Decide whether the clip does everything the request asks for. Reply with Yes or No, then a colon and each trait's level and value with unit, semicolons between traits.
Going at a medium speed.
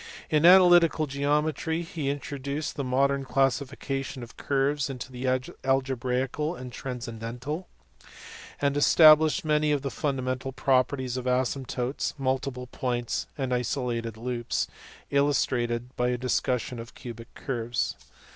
No: slow, 120 wpm